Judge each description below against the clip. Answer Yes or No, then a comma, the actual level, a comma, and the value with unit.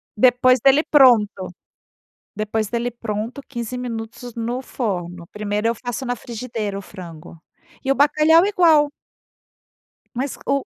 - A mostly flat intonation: No, average, 3.9 semitones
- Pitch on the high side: Yes, high, 240 Hz